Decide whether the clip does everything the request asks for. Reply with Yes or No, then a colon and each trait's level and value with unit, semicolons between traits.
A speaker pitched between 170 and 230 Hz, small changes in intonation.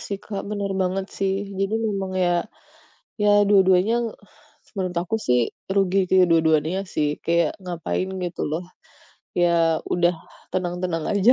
Yes: medium, 185 Hz; narrow, 2.3 semitones